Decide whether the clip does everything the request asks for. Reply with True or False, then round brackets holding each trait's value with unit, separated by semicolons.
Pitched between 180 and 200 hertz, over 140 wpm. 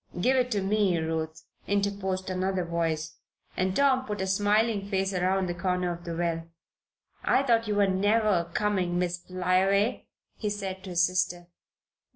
True (190 Hz; 165 wpm)